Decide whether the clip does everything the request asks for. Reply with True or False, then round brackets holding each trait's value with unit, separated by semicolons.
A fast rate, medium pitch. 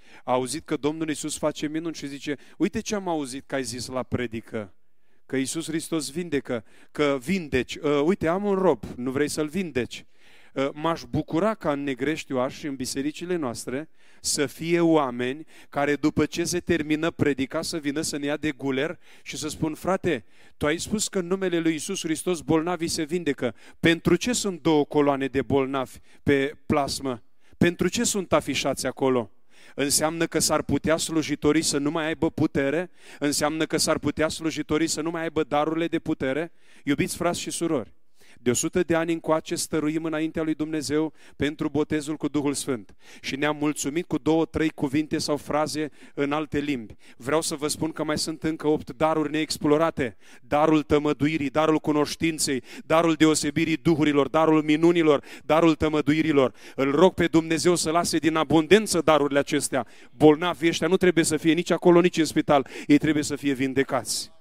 True (175 wpm; 155 Hz)